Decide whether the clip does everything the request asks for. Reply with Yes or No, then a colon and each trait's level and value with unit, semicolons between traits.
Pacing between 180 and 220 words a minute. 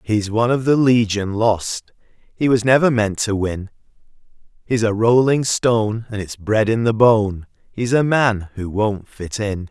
Yes: average, 185 wpm